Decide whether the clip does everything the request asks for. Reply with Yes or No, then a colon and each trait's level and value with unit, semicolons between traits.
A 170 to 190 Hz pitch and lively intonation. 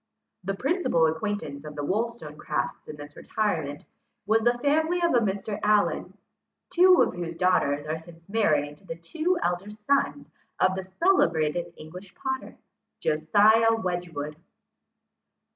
Yes: medium, 185 Hz; wide, 6.4 semitones